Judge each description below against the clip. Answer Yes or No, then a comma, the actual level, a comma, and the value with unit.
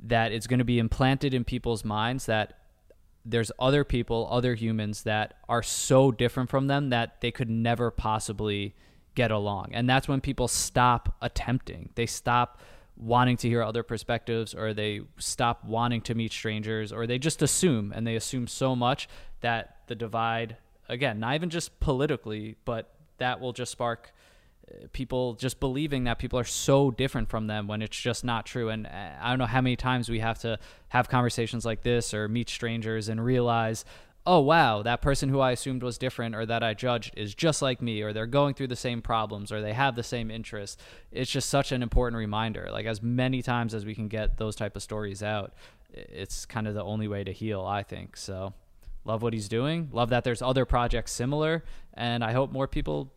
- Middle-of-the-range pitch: No, low, 120 Hz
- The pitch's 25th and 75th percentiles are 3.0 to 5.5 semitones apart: No, narrow, 2.5 semitones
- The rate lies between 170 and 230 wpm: Yes, average, 200 wpm